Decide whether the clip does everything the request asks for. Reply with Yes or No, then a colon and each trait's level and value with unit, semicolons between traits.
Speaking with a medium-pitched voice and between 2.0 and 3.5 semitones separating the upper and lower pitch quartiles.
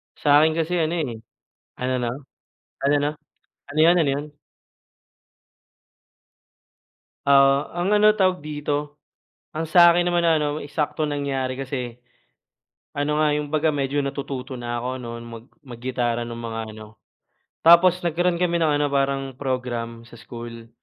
No: medium, 145 Hz; average, 4.1 semitones